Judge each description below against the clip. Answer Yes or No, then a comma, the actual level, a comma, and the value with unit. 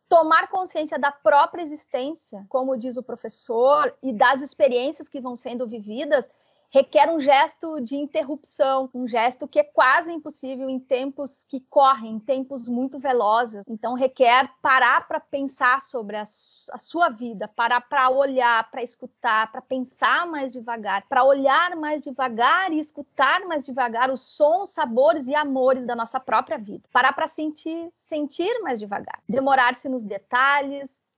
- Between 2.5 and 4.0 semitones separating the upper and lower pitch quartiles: Yes, average, 3.3 semitones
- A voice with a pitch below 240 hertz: No, very high, 270 Hz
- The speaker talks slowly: No, average, 155 wpm